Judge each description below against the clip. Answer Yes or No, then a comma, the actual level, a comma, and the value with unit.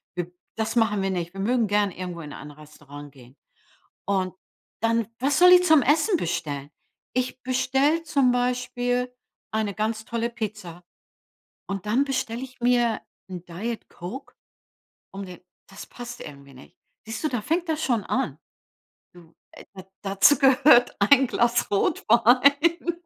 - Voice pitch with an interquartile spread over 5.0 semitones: Yes, wide, 5.6 semitones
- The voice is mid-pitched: No, high, 230 Hz